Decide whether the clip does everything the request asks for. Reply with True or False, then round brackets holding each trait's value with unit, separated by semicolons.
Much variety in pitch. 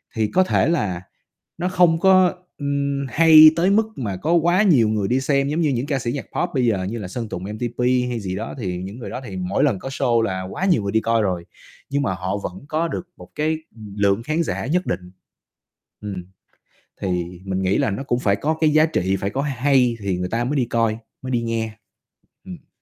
True (7.2 semitones)